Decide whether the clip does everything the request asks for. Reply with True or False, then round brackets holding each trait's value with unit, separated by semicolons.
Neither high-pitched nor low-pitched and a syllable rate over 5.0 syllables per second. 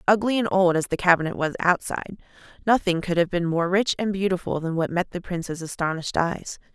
True (180 Hz; 6.0 syllables/s)